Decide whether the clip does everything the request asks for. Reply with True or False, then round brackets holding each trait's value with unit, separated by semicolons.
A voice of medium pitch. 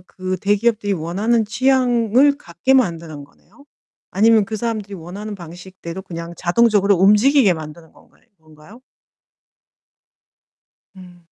False (200 Hz)